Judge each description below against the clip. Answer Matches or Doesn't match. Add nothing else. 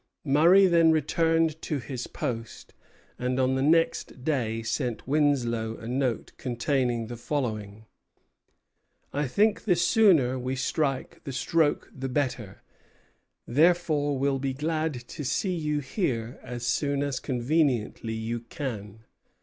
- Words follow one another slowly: Matches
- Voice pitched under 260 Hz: Matches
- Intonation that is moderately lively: Matches